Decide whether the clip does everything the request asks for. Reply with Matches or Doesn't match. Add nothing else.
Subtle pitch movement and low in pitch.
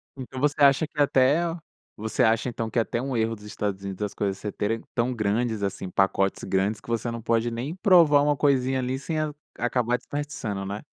Doesn't match